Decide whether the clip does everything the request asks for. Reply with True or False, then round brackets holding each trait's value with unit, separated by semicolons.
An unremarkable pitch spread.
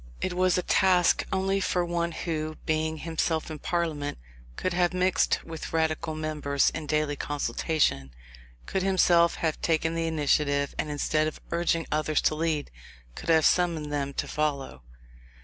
False (2.2 semitones)